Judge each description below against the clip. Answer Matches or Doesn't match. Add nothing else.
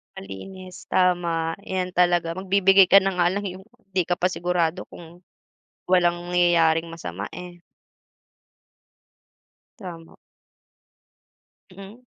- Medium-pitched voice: Matches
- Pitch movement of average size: Doesn't match